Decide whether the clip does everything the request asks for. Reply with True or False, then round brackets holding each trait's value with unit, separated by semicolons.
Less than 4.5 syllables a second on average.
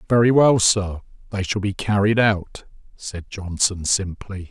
True (4.1 syllables/s)